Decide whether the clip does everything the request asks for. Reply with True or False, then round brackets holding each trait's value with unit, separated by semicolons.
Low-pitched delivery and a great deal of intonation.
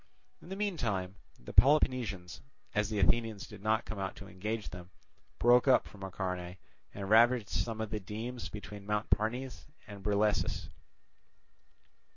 False (105 Hz; 3.3 semitones)